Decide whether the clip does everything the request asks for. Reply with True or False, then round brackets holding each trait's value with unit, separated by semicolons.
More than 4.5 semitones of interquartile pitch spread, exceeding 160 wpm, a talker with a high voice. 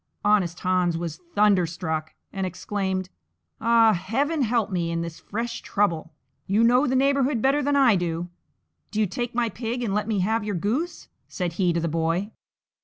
True (5.1 semitones; 180 wpm; 205 Hz)